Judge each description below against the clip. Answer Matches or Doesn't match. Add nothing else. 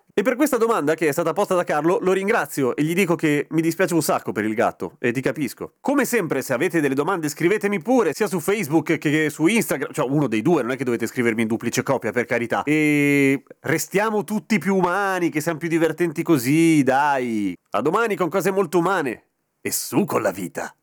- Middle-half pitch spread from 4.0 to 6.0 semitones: Matches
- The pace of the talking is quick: Matches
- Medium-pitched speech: Matches